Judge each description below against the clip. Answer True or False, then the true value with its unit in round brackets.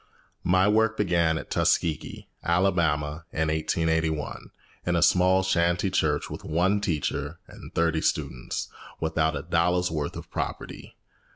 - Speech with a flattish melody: True (2.3 semitones)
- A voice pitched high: False (85 Hz)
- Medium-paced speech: False (130 wpm)